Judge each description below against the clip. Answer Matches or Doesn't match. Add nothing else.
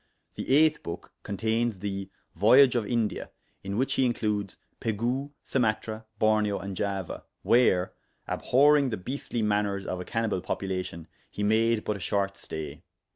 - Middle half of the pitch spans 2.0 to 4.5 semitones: Matches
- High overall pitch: Doesn't match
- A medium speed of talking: Matches